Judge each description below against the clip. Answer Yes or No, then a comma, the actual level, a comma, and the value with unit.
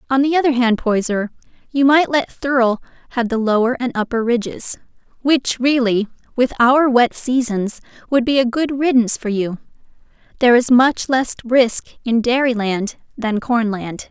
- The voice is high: Yes, high, 245 Hz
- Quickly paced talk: No, average, 165 wpm